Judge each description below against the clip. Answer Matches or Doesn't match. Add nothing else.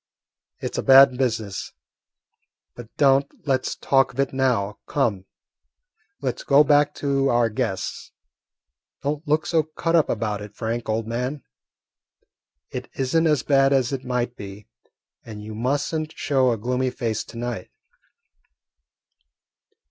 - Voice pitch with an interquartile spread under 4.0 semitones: Matches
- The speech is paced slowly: Doesn't match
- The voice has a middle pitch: Doesn't match